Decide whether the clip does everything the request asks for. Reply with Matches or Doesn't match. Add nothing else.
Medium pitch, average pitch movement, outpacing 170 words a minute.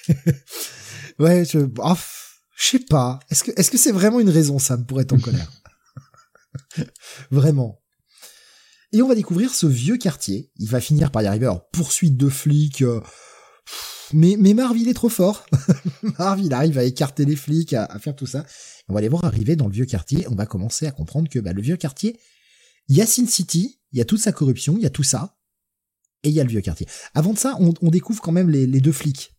Doesn't match